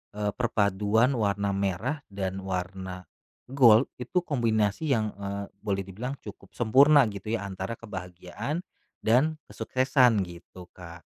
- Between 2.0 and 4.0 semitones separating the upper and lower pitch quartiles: No, average, 4.4 semitones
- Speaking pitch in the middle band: No, low, 105 Hz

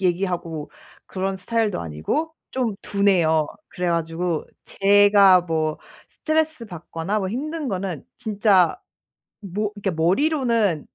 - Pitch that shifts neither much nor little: Yes, average, 4.3 semitones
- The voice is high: Yes, high, 195 Hz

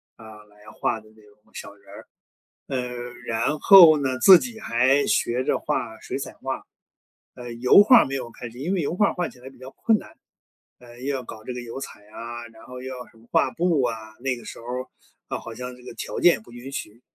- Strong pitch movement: No, average, 2.8 semitones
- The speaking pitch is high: No, low, 125 Hz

